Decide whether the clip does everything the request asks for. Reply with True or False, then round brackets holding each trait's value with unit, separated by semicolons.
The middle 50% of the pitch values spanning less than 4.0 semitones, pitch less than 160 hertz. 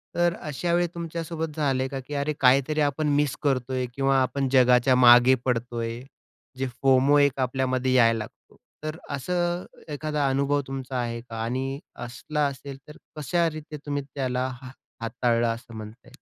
True (2.9 semitones; 135 Hz)